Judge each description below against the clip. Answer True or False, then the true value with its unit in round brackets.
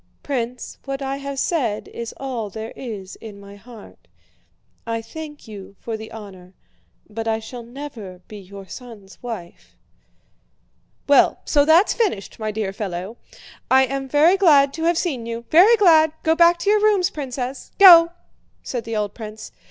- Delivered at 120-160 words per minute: False (170 wpm)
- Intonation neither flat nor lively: False (5.7 semitones)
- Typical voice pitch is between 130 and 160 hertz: False (245 Hz)